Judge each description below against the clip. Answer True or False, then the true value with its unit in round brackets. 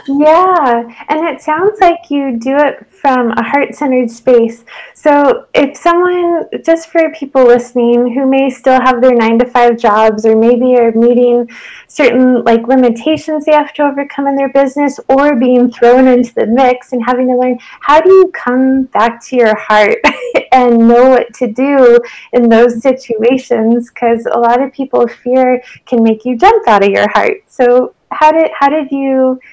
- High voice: True (255 Hz)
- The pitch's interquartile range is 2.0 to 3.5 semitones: True (3.1 semitones)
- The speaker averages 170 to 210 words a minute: True (180 wpm)